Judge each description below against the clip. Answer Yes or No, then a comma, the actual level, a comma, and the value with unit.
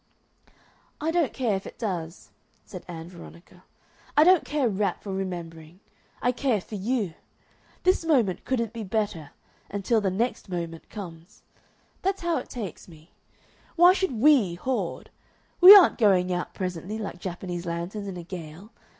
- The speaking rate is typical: Yes, average, 160 wpm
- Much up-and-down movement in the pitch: Yes, wide, 6.1 semitones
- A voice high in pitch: Yes, high, 195 Hz